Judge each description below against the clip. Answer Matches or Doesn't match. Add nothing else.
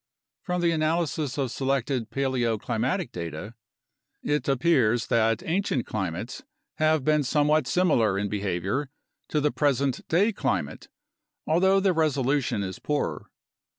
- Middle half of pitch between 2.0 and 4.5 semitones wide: Doesn't match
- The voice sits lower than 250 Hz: Matches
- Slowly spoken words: Matches